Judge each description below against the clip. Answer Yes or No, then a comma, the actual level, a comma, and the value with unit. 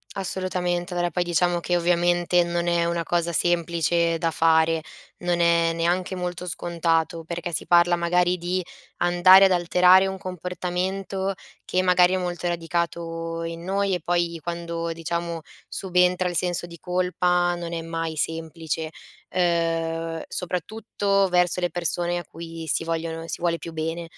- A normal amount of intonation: No, narrow, 1.2 semitones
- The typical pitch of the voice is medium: Yes, medium, 175 Hz